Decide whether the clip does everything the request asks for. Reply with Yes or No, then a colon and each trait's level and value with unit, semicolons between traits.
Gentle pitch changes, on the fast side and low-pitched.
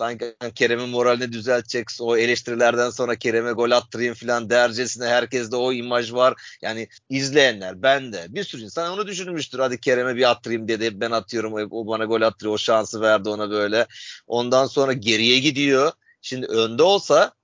Yes: narrow, 2.0 semitones; fast, 170 wpm; low, 120 Hz